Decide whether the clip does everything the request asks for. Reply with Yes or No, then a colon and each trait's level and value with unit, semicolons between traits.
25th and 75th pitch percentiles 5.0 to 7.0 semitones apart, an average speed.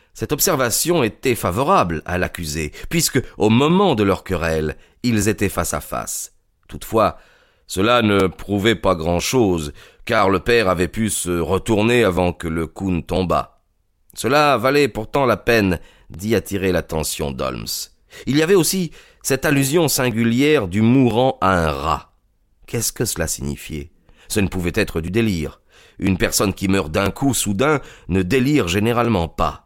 Yes: wide, 5.4 semitones; average, 160 wpm